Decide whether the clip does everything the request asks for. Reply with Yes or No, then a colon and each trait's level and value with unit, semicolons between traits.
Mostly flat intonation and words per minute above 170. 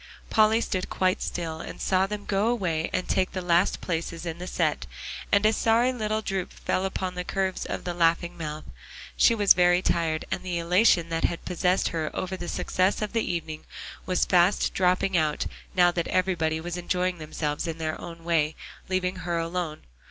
Yes: narrow, 2.2 semitones; average, 190 wpm